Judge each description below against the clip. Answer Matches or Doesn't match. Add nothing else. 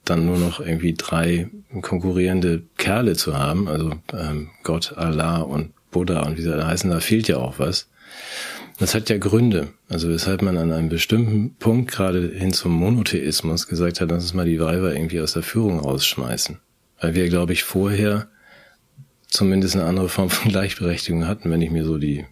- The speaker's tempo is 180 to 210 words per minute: Matches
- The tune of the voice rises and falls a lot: Doesn't match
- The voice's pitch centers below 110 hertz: Matches